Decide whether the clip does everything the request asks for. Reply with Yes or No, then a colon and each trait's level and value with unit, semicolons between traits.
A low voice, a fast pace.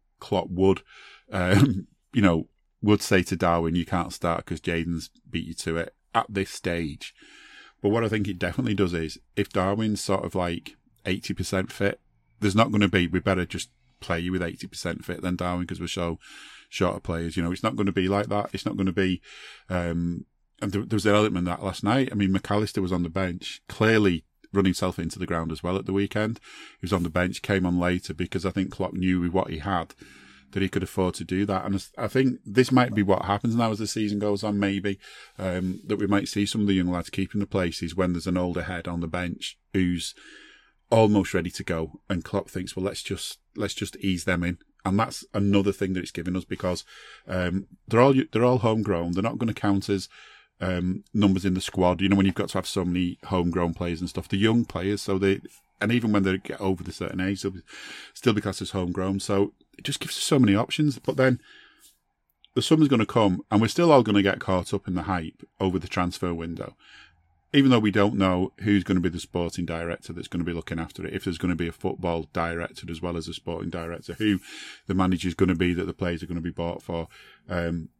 Yes: very low, 95 Hz; fast, 240 wpm